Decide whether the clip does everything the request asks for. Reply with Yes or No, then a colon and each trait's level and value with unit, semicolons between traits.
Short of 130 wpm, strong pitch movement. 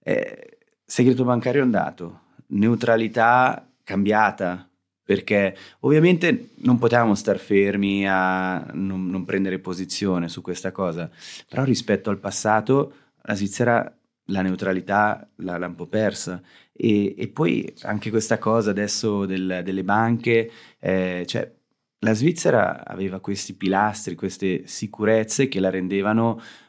No: average, 120 wpm; average, 3.4 semitones